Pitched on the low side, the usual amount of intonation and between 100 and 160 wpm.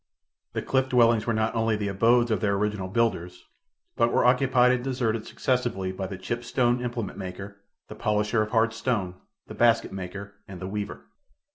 No: low, 110 Hz; average, 3.3 semitones; average, 180 wpm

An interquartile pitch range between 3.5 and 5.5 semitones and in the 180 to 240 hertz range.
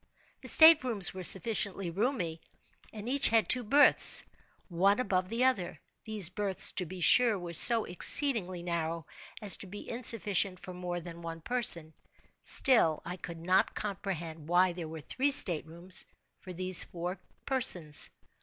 Yes: average, 4.6 semitones; medium, 185 Hz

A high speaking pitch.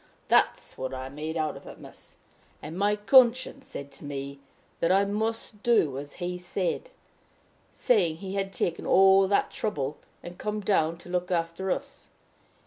No: medium, 180 Hz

